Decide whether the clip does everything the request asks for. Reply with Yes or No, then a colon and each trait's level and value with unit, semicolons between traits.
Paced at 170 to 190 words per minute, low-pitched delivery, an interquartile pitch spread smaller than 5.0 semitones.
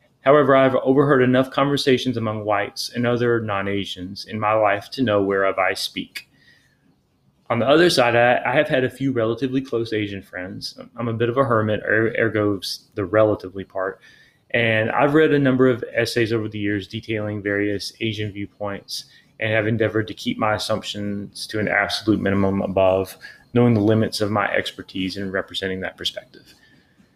Yes: average, 175 wpm; low, 110 Hz; average, 3.4 semitones